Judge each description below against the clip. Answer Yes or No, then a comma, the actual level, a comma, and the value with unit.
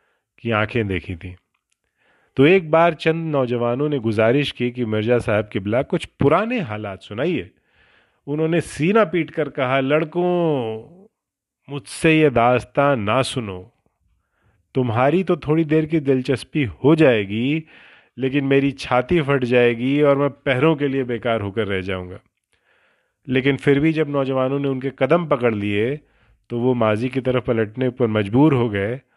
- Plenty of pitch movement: No, average, 4.7 semitones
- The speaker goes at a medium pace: Yes, average, 165 wpm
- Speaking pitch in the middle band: No, low, 130 Hz